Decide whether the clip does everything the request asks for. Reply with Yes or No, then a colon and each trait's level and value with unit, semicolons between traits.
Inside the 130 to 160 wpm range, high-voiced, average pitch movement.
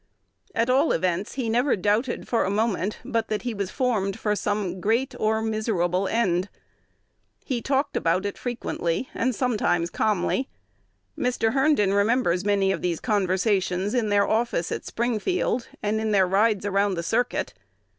Yes: average, 155 wpm; high, 210 Hz; average, 3.6 semitones